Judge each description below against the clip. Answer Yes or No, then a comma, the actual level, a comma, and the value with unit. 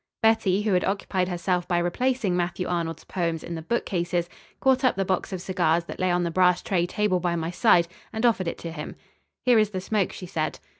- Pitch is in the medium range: Yes, medium, 180 Hz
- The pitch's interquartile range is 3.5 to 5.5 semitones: No, average, 2.7 semitones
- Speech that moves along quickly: Yes, fast, 220 wpm